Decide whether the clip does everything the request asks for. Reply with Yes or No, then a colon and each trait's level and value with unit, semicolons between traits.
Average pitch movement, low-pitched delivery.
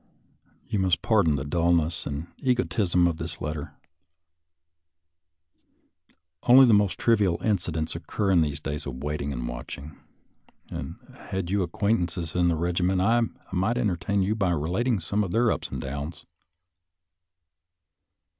Yes: average, 4.5 semitones; very low, 90 Hz